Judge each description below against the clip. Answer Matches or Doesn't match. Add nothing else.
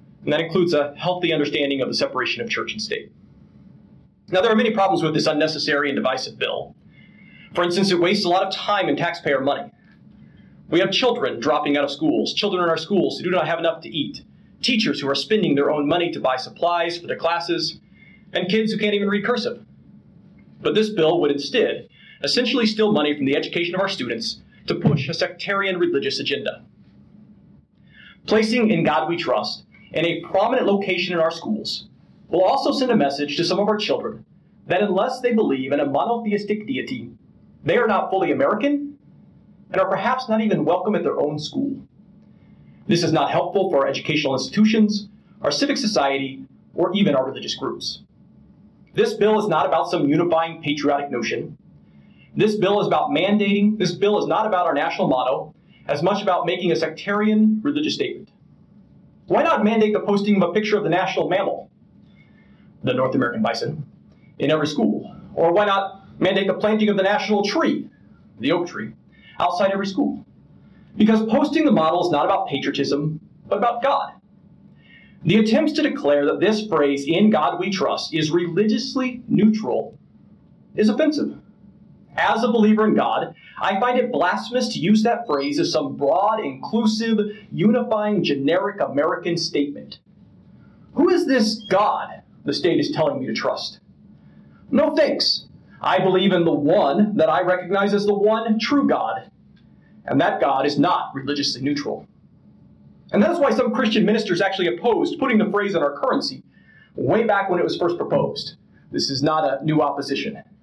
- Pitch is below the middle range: Doesn't match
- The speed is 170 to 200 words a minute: Matches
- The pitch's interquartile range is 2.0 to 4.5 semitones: Doesn't match